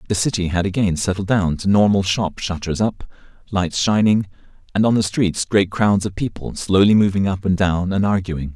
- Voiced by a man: Yes, male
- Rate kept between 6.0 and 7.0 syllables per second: No, 5.1 syllables/s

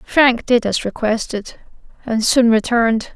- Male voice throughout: No, female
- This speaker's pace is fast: No, slow, 135 wpm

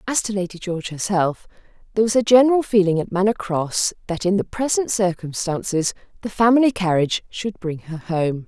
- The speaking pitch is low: No, high, 195 Hz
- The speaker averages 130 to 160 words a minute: No, average, 175 wpm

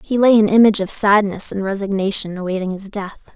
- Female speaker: Yes, female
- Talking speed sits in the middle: Yes, average, 195 wpm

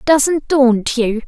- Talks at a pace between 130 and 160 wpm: Yes, average, 140 wpm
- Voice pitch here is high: Yes, very high, 260 Hz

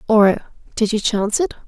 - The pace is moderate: Yes, average, 145 wpm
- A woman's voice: Yes, female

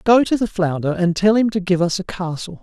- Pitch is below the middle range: No, high, 190 Hz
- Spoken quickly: Yes, fast, 275 wpm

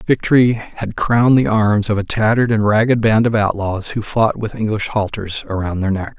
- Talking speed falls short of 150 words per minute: No, fast, 205 wpm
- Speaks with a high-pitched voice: No, low, 110 Hz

